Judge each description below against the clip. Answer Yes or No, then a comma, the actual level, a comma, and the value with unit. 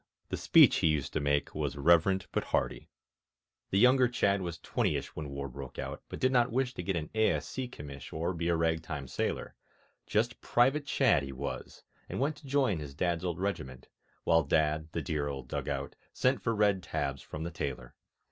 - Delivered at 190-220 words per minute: Yes, average, 200 wpm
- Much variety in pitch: Yes, wide, 7.3 semitones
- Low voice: Yes, very low, 85 Hz